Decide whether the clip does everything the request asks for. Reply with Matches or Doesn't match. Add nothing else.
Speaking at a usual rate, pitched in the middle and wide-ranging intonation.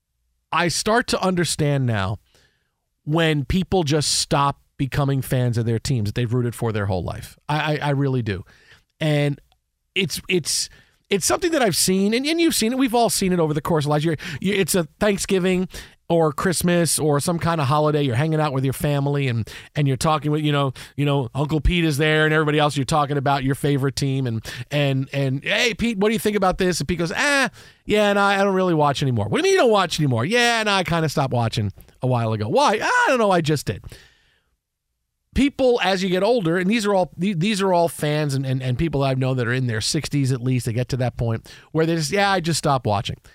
Doesn't match